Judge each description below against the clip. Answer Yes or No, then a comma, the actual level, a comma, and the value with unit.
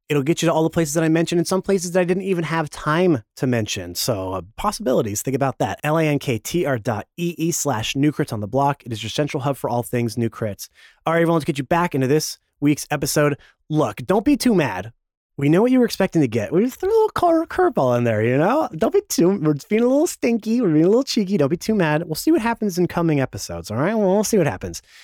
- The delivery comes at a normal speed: No, fast, 285 wpm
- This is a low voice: No, medium, 155 Hz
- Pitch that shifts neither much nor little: No, wide, 6.3 semitones